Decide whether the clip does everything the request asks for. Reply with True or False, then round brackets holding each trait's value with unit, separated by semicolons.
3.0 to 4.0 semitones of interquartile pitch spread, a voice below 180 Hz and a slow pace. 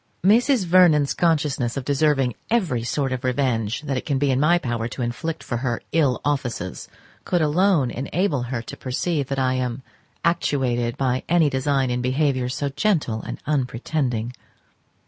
False (3.7 semitones; 135 Hz; 165 wpm)